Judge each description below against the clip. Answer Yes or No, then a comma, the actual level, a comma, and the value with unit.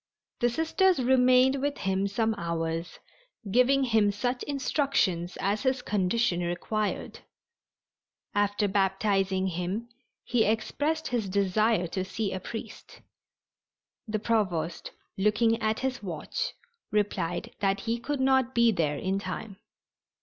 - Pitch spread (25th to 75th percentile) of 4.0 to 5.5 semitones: Yes, average, 4.5 semitones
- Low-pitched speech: No, high, 210 Hz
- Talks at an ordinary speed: No, slow, 120 wpm